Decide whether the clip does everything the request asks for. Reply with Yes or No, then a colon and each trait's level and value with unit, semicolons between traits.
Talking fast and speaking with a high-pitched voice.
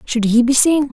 Yes: fast, 240 wpm; very high, 255 Hz